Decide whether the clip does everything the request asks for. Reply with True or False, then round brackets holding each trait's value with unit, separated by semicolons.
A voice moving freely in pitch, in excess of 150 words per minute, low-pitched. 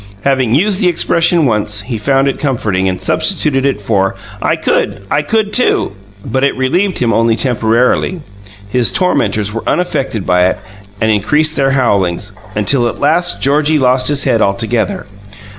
True (5.8 semitones; 160 wpm; 125 Hz)